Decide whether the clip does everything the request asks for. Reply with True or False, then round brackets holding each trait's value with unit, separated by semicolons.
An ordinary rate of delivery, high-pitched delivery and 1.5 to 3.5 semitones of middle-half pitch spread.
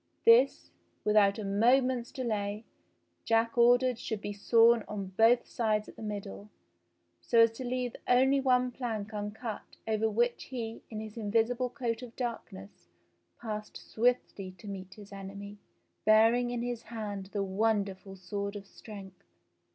True (150 wpm; 220 Hz; 2.9 semitones)